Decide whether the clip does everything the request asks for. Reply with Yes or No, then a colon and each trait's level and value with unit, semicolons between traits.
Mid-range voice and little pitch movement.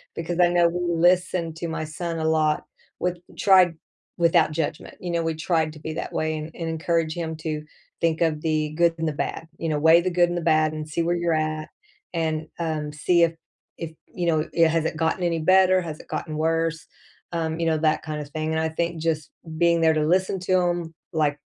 Yes: medium, 165 Hz; narrow, 1.5 semitones